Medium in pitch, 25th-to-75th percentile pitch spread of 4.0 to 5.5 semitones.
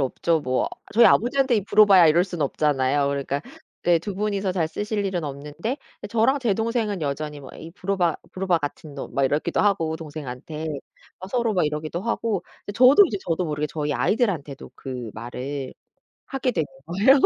No: medium, 170 Hz; wide, 5.9 semitones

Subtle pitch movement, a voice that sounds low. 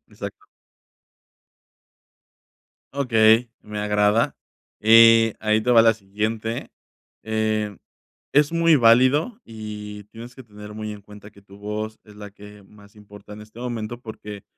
Yes: narrow, 1.7 semitones; low, 110 Hz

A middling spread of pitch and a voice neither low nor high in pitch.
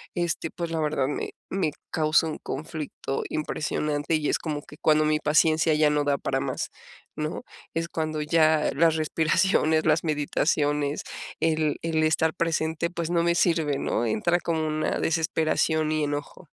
No: narrow, 1.3 semitones; medium, 155 Hz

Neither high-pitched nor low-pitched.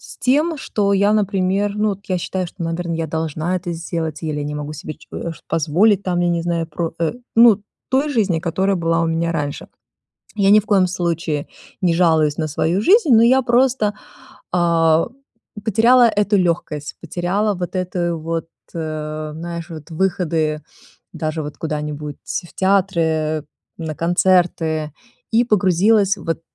Yes: medium, 175 Hz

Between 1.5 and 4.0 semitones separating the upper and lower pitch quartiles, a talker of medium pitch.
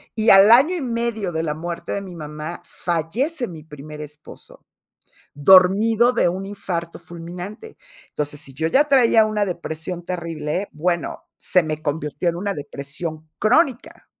No: wide, 5.4 semitones; medium, 175 Hz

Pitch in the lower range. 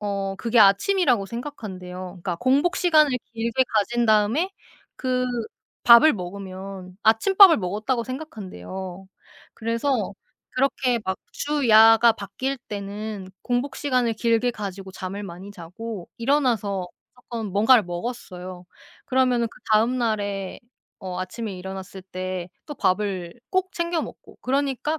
No: high, 220 Hz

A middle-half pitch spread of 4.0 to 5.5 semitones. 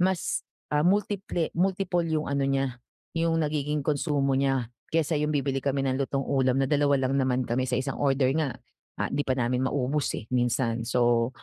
No: average, 2.7 semitones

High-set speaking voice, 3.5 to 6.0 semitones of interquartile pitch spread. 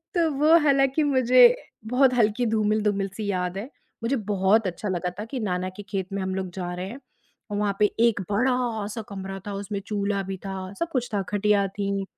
Yes: high, 205 Hz; average, 3.9 semitones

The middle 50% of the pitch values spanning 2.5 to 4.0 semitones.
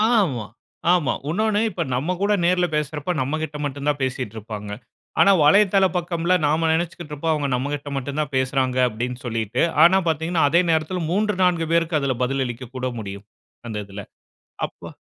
No: average, 5.1 semitones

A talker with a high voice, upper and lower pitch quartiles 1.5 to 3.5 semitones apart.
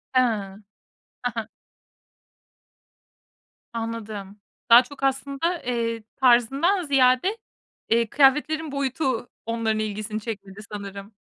No: high, 240 Hz; average, 4.2 semitones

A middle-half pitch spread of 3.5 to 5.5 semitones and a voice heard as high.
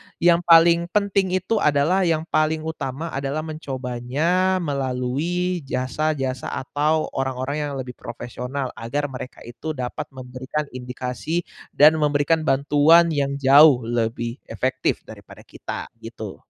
No: average, 3.8 semitones; medium, 145 Hz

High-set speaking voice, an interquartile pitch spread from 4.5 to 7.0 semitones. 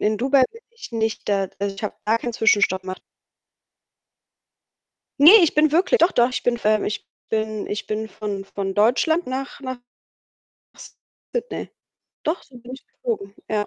Yes: high, 230 Hz; average, 5.3 semitones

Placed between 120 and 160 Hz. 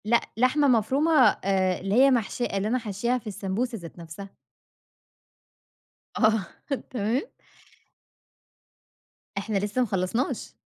No: high, 220 Hz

